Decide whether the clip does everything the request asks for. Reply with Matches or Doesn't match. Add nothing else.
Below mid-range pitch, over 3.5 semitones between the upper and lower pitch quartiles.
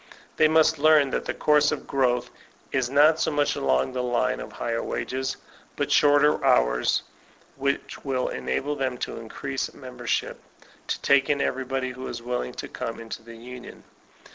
Doesn't match